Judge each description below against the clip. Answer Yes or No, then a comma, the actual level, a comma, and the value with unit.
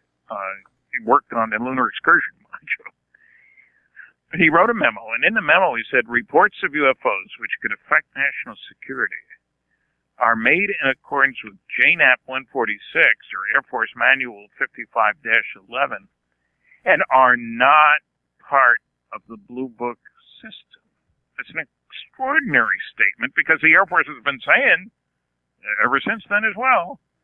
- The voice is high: No, low, 135 Hz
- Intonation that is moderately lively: No, wide, 8.3 semitones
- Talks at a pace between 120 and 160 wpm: Yes, average, 140 wpm